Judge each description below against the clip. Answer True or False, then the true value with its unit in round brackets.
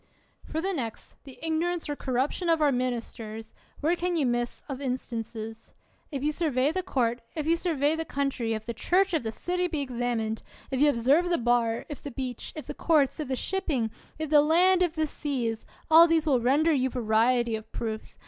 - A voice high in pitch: True (275 Hz)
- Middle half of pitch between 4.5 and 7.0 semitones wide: True (5.1 semitones)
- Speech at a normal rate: False (210 wpm)